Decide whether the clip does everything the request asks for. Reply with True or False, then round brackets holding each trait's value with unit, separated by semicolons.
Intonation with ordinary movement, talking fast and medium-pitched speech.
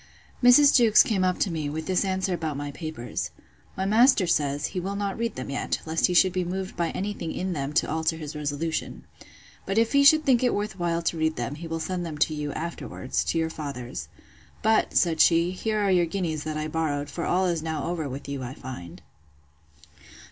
True (3.9 semitones; 220 wpm; 165 Hz)